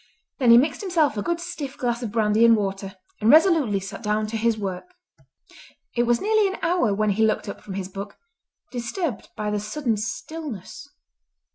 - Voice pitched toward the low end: No, high, 230 Hz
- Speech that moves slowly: No, average, 185 wpm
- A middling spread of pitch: No, wide, 6.4 semitones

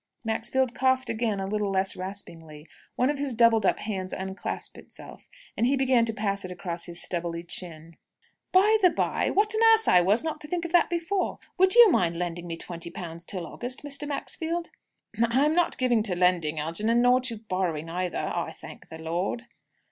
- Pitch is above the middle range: Yes, high, 215 Hz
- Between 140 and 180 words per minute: No, average, 195 wpm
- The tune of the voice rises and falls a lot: Yes, wide, 7.2 semitones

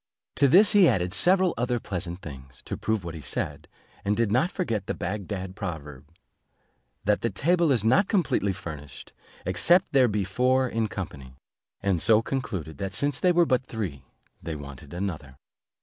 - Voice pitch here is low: Yes, low, 100 Hz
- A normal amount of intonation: No, wide, 7.3 semitones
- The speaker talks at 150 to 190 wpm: Yes, average, 170 wpm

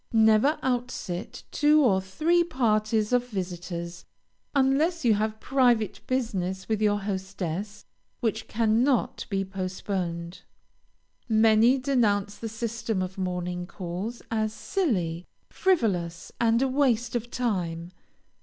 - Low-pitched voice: No, high, 215 Hz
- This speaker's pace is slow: Yes, slow, 115 wpm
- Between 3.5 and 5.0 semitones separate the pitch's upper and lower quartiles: Yes, average, 4.5 semitones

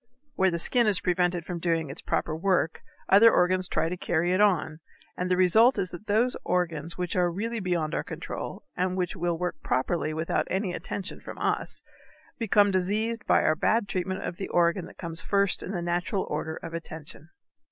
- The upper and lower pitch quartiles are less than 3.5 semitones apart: Yes, average, 2.7 semitones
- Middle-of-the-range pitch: Yes, medium, 180 Hz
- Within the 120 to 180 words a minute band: No, average, 195 wpm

